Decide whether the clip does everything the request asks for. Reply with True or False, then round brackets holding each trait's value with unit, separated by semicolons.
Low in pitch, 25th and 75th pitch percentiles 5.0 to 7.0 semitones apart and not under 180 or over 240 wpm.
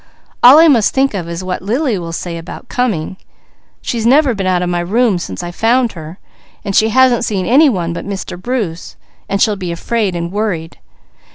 False (200 Hz; 5.6 semitones; 200 wpm)